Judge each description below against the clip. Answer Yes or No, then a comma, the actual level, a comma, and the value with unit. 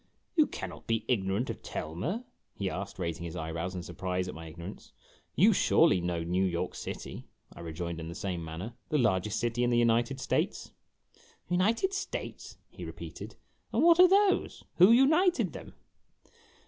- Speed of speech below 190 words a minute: Yes, average, 180 wpm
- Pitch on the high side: No, very low, 95 Hz